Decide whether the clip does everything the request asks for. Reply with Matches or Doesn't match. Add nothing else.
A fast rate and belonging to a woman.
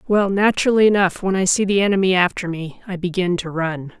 Matches